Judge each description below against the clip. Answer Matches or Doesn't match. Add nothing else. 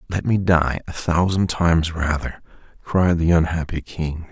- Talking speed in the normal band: Matches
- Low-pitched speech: Matches